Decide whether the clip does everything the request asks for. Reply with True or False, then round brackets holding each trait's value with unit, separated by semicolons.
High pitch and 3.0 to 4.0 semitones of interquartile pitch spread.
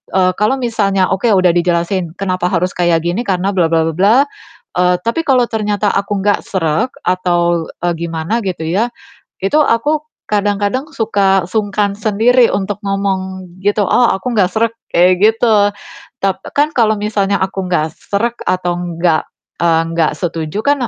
True (195 Hz; 3.5 semitones)